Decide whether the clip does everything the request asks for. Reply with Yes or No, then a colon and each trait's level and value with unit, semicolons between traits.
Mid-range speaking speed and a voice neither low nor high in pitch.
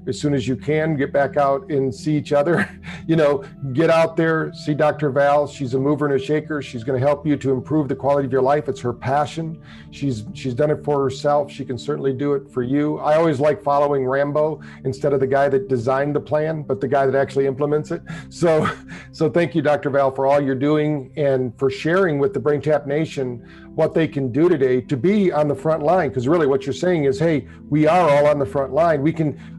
No: fast, 240 wpm; medium, 145 Hz